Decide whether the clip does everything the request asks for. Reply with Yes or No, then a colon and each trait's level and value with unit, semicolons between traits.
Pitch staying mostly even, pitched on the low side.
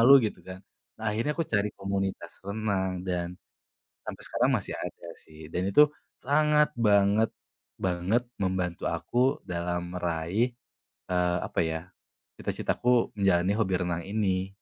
No: average, 3.9 semitones; very low, 95 Hz